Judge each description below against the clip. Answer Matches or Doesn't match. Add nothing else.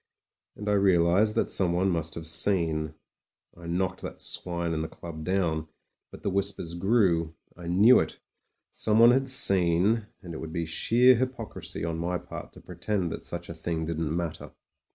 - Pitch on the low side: Matches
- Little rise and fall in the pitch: Doesn't match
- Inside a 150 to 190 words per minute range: Matches